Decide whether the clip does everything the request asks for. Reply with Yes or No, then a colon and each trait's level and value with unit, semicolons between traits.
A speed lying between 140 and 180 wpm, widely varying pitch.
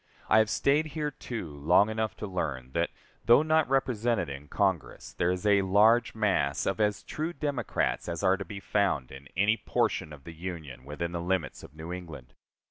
No: average, 195 wpm; wide, 5.7 semitones